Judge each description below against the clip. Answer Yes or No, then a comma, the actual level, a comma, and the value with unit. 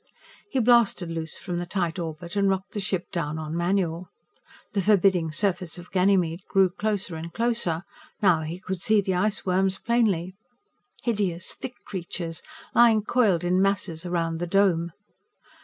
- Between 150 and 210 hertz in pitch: Yes, medium, 185 Hz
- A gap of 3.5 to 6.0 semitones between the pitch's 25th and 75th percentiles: No, average, 2.9 semitones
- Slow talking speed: No, average, 155 wpm